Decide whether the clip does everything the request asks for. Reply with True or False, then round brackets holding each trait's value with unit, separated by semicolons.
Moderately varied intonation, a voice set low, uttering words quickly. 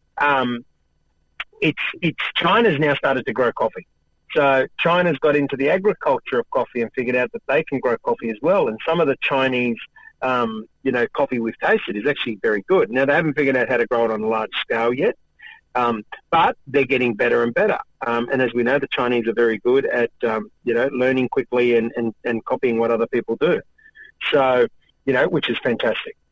True (4.3 semitones; 125 Hz; 210 wpm)